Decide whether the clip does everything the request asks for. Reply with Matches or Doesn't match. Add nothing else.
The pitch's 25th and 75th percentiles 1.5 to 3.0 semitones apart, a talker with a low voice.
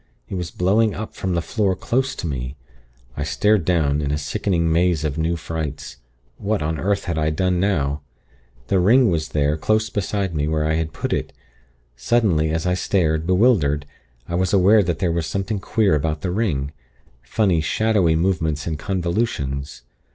Doesn't match